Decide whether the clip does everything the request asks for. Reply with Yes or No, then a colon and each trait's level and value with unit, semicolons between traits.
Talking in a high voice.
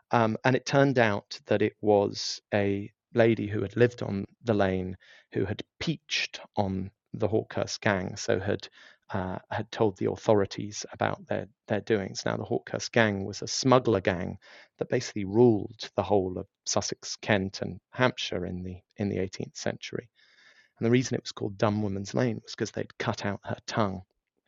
No: low, 105 Hz